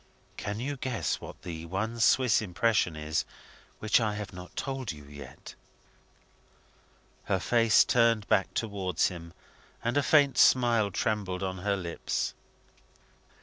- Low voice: Yes, low, 105 Hz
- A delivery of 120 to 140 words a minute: Yes, slow, 135 wpm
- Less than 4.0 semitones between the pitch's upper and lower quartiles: No, average, 4.5 semitones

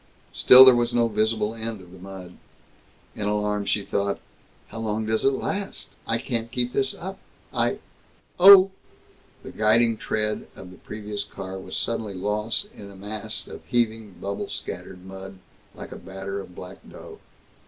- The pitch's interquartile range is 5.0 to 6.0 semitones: No, average, 2.9 semitones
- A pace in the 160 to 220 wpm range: Yes, average, 165 wpm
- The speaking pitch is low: Yes, low, 105 Hz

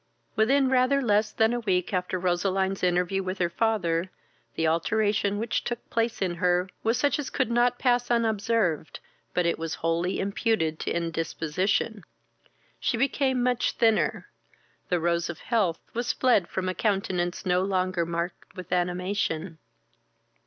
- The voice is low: No, high, 190 Hz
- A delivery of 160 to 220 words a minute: No, average, 150 wpm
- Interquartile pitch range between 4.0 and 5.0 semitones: Yes, average, 4.5 semitones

